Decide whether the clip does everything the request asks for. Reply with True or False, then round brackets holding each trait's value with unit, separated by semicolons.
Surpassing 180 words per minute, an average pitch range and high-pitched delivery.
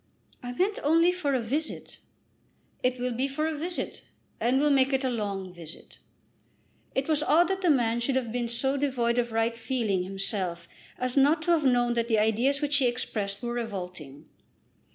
True (190 wpm; 4.0 semitones; 245 Hz)